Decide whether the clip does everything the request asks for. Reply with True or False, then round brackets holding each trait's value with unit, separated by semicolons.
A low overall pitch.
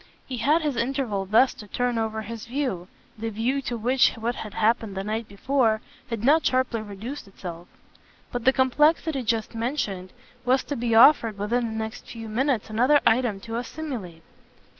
False (230 Hz)